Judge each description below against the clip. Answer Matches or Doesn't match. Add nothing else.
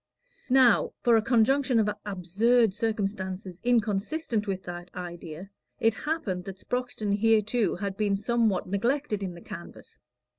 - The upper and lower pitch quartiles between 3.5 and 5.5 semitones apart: Matches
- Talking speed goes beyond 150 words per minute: Doesn't match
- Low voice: Doesn't match